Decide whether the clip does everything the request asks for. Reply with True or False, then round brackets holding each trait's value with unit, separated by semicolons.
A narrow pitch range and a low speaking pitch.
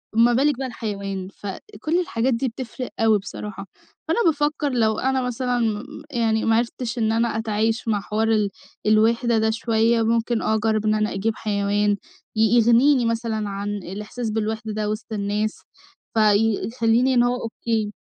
False (2.0 semitones; 225 Hz)